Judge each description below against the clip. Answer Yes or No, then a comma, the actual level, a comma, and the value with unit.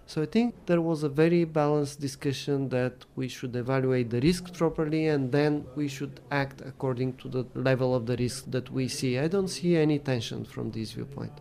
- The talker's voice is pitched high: No, medium, 140 Hz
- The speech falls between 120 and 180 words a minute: No, fast, 205 wpm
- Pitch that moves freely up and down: No, average, 3.4 semitones